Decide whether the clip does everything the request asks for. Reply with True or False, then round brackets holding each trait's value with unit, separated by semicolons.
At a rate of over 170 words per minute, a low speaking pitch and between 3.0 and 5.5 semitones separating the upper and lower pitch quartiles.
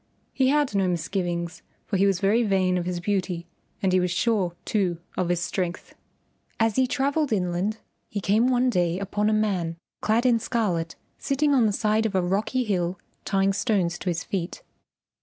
False (185 wpm; 195 Hz; 3.9 semitones)